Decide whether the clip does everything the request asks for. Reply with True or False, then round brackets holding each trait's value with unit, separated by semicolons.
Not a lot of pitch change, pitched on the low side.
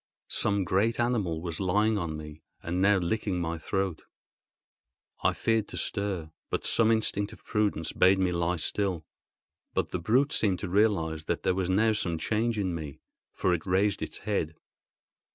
False (4.0 semitones; 95 Hz)